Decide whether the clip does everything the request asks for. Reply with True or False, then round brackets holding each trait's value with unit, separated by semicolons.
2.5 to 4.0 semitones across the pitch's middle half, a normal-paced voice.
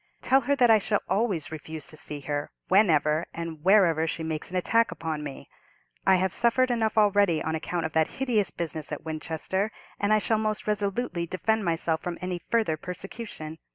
False (5.1 semitones; 190 wpm)